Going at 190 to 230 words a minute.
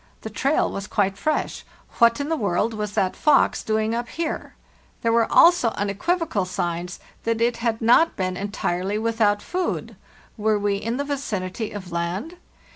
No: average, 165 wpm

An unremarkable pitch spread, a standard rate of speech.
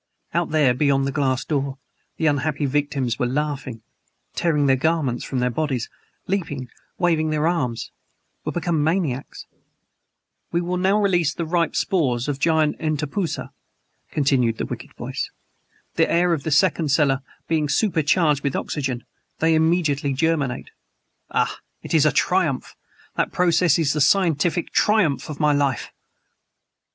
Yes: average, 3.4 semitones; average, 145 wpm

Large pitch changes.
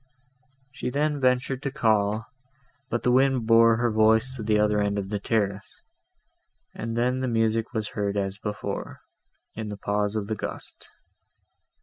No: average, 2.9 semitones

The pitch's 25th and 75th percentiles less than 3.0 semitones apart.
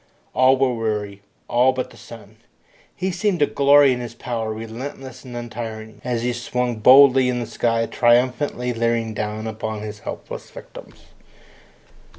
Yes: narrow, 2.6 semitones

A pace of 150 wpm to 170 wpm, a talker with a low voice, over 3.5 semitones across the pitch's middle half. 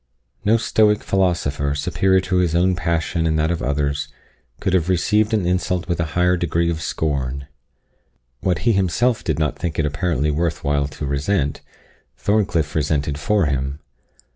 Yes: average, 165 wpm; very low, 85 Hz; average, 4.1 semitones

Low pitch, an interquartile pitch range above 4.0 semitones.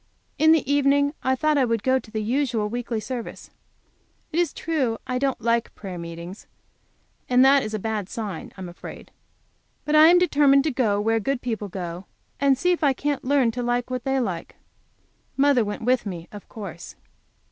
No: high, 245 Hz; average, 4.7 semitones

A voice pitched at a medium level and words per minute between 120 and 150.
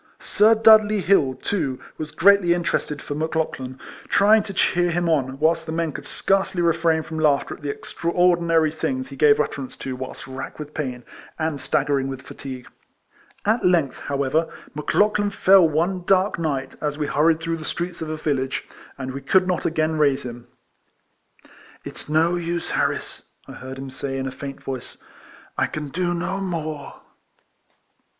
No: medium, 155 Hz; average, 180 wpm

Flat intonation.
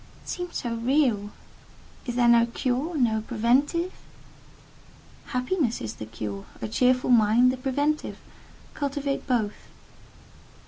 No: average, 3.8 semitones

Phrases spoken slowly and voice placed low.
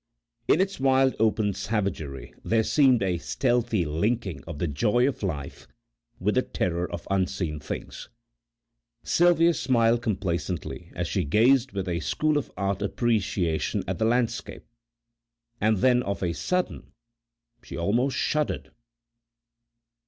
Yes: slow, 130 wpm; low, 105 Hz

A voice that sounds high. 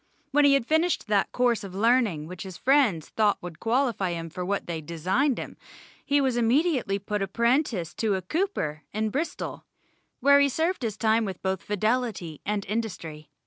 Yes: high, 215 Hz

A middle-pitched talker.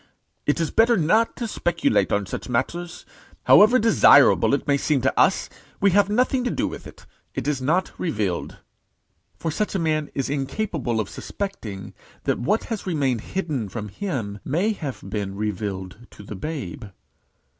Yes: medium, 150 Hz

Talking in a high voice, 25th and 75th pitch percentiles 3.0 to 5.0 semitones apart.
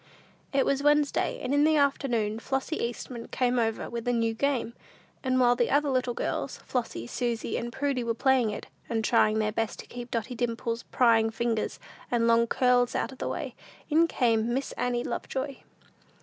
No: high, 245 Hz; narrow, 2.6 semitones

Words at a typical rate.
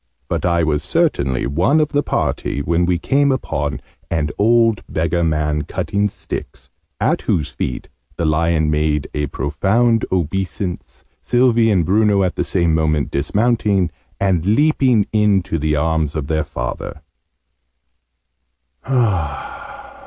No: slow, 130 wpm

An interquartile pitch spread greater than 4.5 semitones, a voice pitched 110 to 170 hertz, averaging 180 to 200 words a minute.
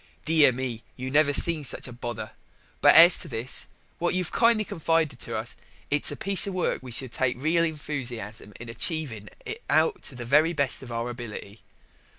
Yes: wide, 5.5 semitones; low, 135 Hz; average, 195 wpm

